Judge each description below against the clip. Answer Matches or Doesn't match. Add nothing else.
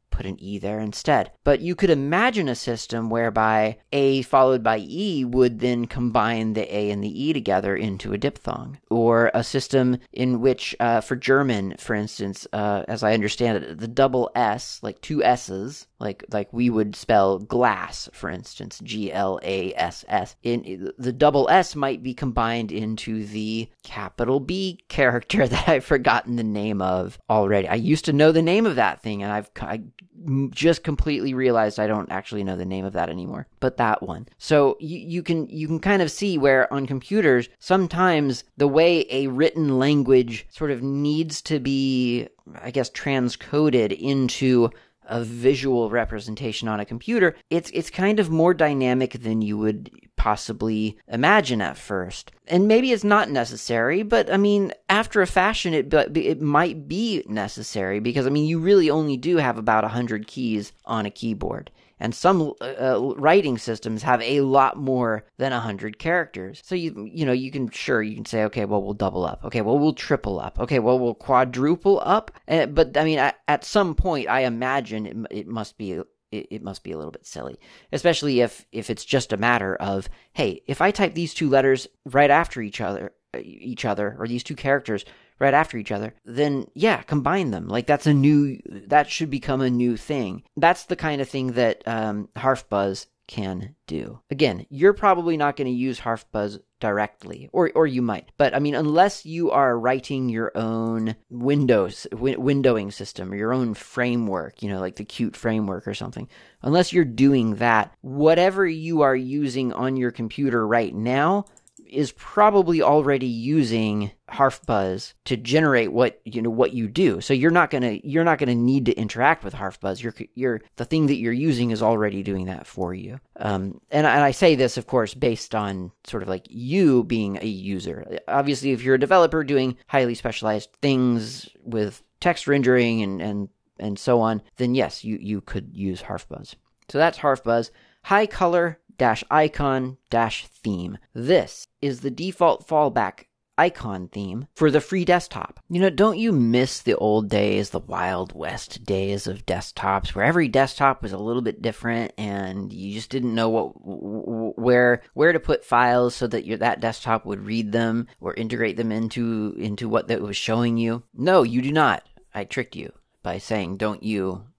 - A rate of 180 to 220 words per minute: Matches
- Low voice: Matches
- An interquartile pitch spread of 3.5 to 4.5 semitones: Doesn't match